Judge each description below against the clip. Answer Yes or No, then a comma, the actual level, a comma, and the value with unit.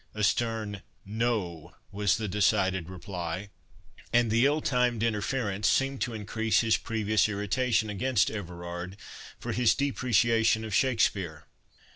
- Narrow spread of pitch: No, average, 3.3 semitones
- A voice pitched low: Yes, low, 110 Hz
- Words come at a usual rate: No, slow, 125 wpm